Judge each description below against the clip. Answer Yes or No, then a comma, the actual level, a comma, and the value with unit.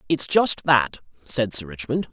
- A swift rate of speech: No, average, 170 wpm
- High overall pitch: No, low, 130 Hz